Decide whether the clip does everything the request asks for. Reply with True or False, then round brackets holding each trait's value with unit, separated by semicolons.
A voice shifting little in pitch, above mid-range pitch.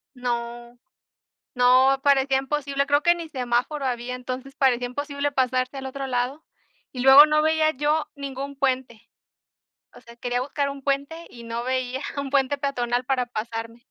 True (2.3 semitones; 265 Hz)